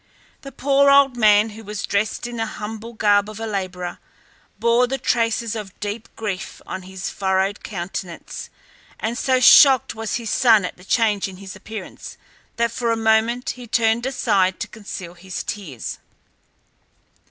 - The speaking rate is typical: Yes, average, 165 wpm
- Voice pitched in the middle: No, high, 220 Hz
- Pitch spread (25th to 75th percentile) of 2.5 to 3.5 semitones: Yes, average, 3.1 semitones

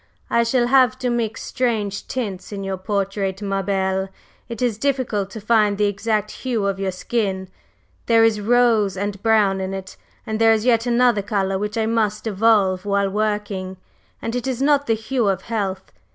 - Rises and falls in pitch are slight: No, average, 3.0 semitones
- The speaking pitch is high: Yes, high, 210 Hz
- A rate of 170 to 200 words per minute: Yes, average, 185 wpm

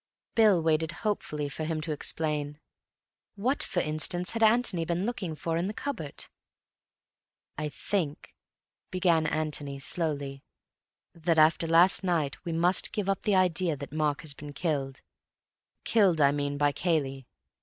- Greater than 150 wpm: No, average, 145 wpm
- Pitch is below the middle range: No, medium, 160 Hz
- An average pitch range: Yes, average, 3.6 semitones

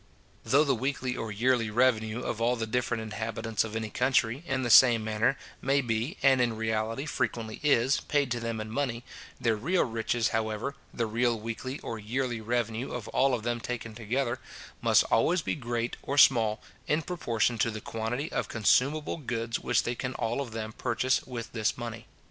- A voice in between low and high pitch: No, low, 120 Hz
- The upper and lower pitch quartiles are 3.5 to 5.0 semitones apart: No, narrow, 2.5 semitones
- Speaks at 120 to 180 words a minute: No, average, 190 wpm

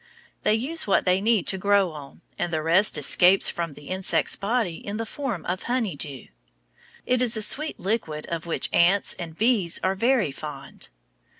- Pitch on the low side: No, high, 190 Hz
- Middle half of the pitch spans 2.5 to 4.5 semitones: No, average, 5.1 semitones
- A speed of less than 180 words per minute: No, average, 185 wpm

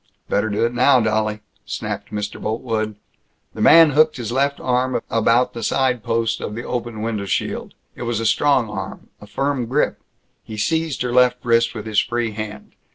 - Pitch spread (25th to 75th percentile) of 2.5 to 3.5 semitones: Yes, average, 2.8 semitones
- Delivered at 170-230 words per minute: Yes, average, 185 wpm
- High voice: No, low, 115 Hz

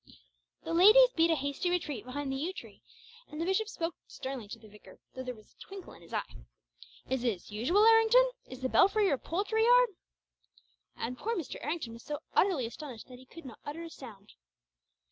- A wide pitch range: Yes, wide, 7.4 semitones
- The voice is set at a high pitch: Yes, very high, 300 Hz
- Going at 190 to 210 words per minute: Yes, average, 200 wpm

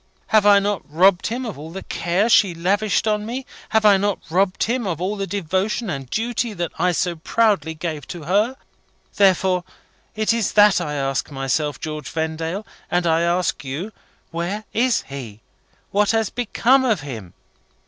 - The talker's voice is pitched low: No, medium, 185 Hz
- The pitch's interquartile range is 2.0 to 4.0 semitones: No, average, 4.8 semitones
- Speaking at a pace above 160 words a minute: Yes, average, 180 wpm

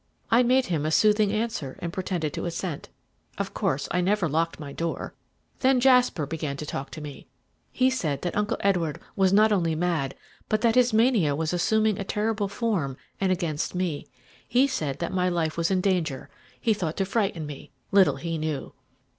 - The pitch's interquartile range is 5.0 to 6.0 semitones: Yes, wide, 5.4 semitones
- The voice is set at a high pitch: No, medium, 180 Hz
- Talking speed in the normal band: Yes, average, 190 wpm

